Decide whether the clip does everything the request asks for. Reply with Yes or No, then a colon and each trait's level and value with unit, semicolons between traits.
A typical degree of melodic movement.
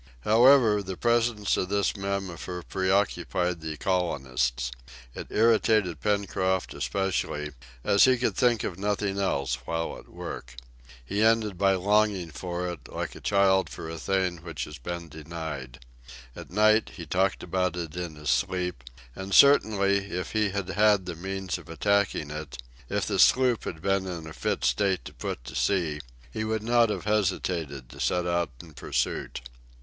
Yes: average, 3.8 semitones